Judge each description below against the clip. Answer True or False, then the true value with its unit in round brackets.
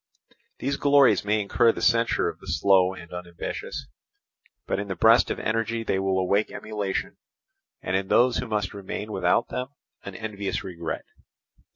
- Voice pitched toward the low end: True (100 Hz)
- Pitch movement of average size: True (3.1 semitones)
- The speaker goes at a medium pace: True (165 wpm)